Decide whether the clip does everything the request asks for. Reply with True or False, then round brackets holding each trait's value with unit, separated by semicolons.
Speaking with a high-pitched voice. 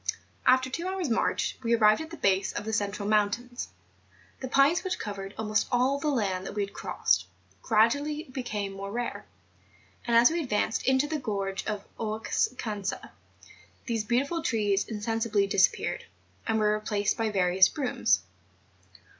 True (220 Hz)